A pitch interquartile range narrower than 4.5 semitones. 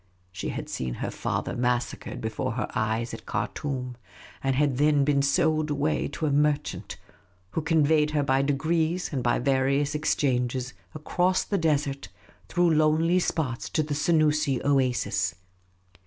Yes: average, 3.3 semitones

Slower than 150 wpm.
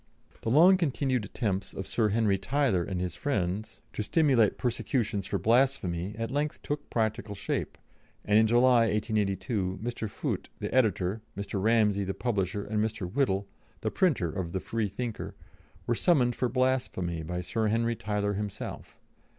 No: average, 155 wpm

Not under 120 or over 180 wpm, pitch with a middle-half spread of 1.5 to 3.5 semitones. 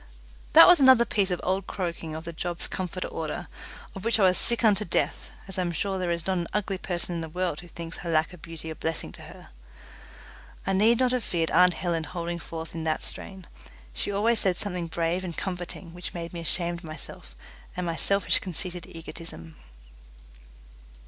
No: fast, 205 wpm; narrow, 2.5 semitones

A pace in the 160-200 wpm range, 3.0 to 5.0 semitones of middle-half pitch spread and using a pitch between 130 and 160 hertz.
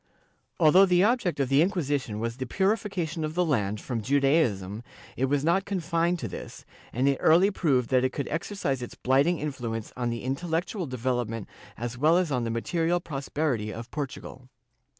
No: average, 180 wpm; wide, 5.5 semitones; medium, 140 Hz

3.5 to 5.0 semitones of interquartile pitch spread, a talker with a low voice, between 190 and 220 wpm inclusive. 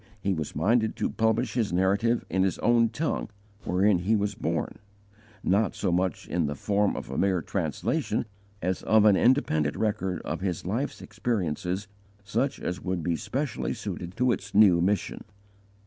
No: average, 3.8 semitones; low, 100 Hz; average, 165 wpm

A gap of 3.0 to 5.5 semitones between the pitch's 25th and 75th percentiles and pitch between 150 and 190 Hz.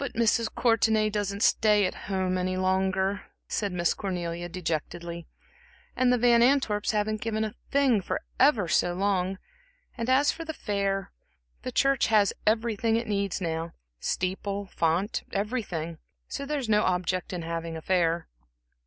No: average, 3.8 semitones; high, 200 Hz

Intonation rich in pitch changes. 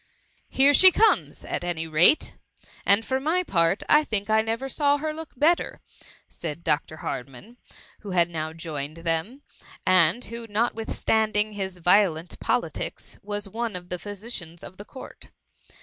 Yes: wide, 6.0 semitones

